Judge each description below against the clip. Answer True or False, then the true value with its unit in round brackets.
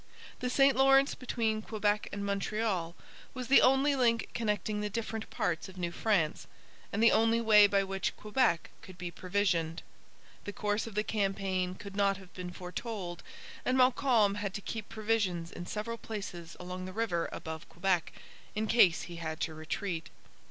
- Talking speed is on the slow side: False (170 wpm)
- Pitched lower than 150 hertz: False (205 Hz)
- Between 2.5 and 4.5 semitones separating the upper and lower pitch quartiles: True (3.9 semitones)